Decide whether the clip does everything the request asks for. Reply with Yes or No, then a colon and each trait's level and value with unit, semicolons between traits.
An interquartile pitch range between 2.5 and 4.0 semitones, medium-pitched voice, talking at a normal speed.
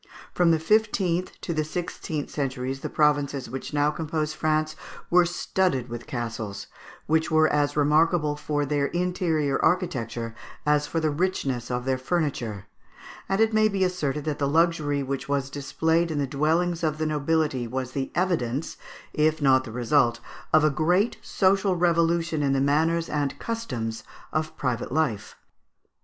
Yes: average, 3.7 semitones; medium, 150 Hz; average, 160 wpm